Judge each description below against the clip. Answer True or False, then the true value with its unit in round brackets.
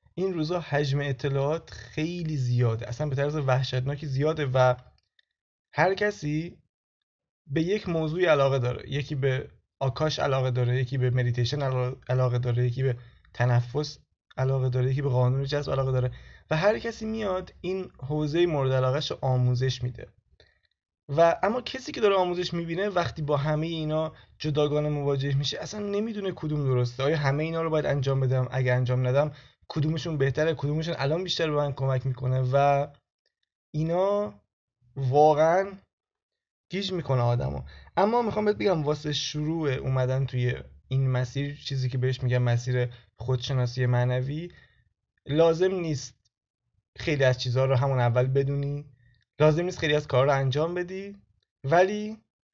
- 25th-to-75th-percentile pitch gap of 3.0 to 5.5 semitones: True (4.1 semitones)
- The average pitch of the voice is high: False (140 Hz)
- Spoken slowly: False (145 wpm)